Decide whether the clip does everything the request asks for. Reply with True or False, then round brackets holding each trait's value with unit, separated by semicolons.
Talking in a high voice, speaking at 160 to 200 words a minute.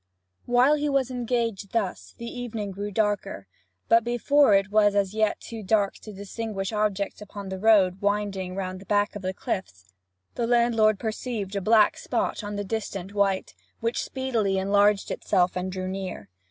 True (205 Hz; 170 wpm)